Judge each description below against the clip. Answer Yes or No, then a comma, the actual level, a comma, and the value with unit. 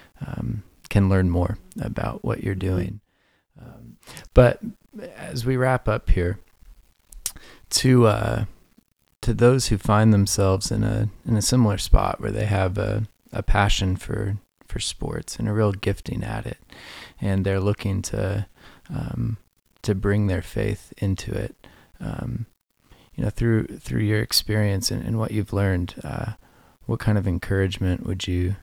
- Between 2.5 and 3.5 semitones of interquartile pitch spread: Yes, average, 3.1 semitones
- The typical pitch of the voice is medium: No, low, 105 Hz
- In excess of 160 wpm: No, average, 155 wpm